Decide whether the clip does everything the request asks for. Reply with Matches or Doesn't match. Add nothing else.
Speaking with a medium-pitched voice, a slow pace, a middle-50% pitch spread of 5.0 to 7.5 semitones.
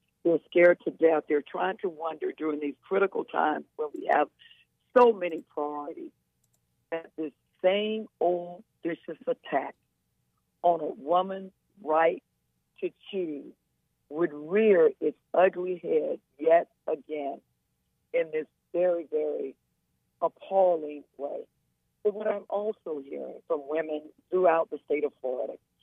Matches